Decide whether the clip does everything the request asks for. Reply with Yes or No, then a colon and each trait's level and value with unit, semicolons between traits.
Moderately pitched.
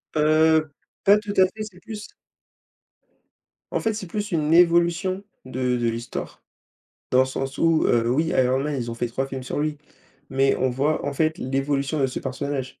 Yes: medium, 145 Hz